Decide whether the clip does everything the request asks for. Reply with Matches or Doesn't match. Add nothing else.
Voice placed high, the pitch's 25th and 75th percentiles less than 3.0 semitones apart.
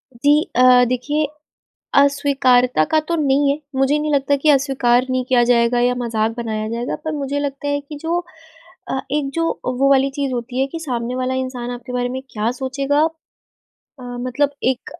Matches